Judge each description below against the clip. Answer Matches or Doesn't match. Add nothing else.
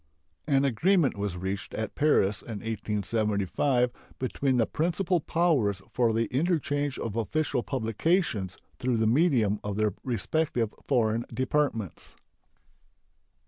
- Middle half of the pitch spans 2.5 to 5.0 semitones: Doesn't match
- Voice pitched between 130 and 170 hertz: Doesn't match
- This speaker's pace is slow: Matches